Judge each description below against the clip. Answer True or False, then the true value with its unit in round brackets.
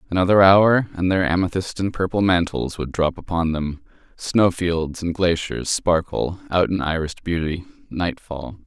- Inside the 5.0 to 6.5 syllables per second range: False (4.6 syllables/s)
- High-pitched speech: False (85 Hz)